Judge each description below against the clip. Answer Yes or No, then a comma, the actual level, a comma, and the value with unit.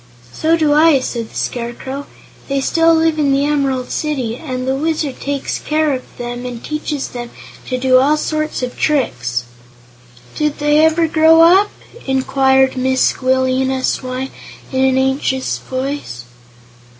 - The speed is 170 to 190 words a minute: No, average, 150 wpm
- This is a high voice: Yes, very high, 270 Hz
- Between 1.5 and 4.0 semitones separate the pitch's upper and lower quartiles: Yes, average, 2.9 semitones